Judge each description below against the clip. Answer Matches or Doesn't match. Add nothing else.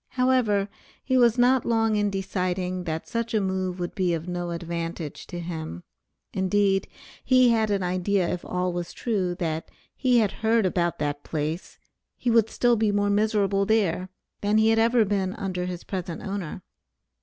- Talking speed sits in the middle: Matches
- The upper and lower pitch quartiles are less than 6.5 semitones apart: Matches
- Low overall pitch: Doesn't match